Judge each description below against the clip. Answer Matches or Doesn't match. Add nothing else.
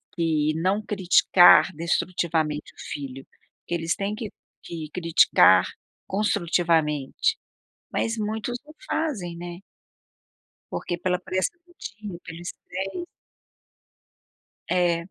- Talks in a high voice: Doesn't match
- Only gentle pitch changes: Doesn't match